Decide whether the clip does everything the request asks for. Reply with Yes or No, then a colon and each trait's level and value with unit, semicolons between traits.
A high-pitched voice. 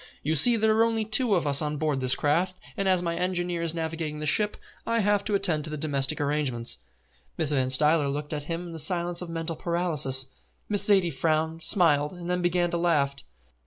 No: medium, 165 Hz